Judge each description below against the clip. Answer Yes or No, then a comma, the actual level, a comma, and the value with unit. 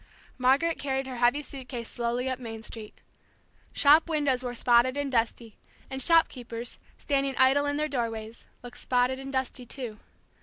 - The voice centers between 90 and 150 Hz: No, very high, 255 Hz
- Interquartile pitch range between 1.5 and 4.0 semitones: Yes, narrow, 2.5 semitones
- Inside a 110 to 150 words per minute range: No, average, 160 wpm